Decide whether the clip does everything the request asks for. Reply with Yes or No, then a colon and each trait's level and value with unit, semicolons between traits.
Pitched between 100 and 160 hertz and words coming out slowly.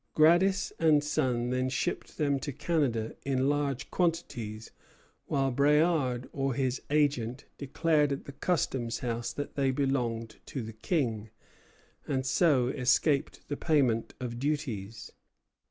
Yes: low, 135 Hz; slow, 130 wpm